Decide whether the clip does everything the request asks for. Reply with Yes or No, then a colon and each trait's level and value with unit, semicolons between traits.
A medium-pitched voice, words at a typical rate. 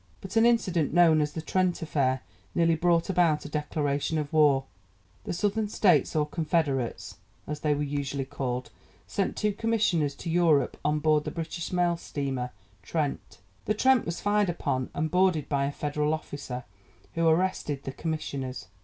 Yes: medium, 155 Hz; average, 165 wpm